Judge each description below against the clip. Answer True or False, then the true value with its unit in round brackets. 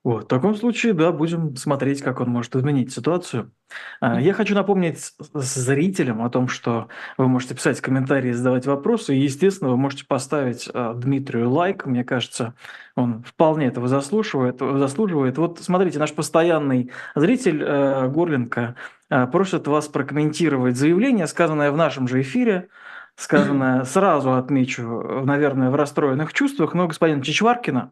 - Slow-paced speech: False (145 wpm)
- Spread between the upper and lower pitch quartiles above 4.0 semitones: True (4.6 semitones)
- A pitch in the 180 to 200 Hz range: False (140 Hz)